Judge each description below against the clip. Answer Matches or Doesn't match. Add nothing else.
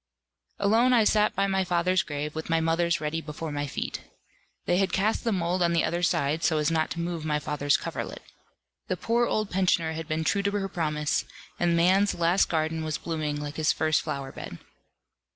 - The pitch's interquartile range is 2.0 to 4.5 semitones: Matches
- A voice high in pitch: Doesn't match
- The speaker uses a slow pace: Doesn't match